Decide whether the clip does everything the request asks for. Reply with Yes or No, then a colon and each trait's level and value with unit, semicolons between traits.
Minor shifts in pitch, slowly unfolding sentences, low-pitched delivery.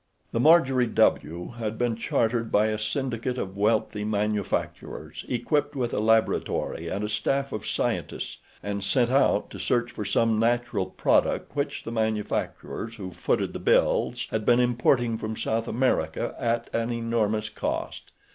No: narrow, 2.3 semitones; average, 155 wpm; low, 115 Hz